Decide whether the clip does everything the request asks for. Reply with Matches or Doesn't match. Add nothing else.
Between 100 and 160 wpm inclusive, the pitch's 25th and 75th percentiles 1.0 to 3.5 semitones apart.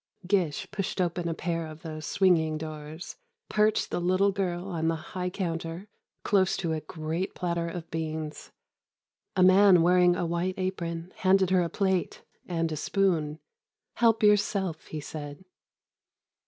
Matches